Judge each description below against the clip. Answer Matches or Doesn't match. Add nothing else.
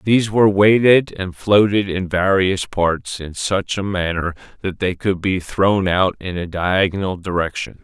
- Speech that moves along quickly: Doesn't match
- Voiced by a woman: Doesn't match